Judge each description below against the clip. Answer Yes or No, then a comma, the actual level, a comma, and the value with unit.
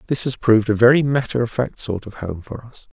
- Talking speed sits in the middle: No, fast, 260 wpm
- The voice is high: No, low, 115 Hz